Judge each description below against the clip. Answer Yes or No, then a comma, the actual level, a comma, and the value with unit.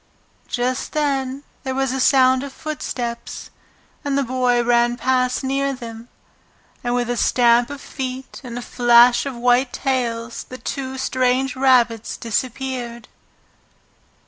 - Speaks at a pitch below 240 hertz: No, very high, 255 Hz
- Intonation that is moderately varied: No, narrow, 1.8 semitones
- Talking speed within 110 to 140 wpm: Yes, slow, 135 wpm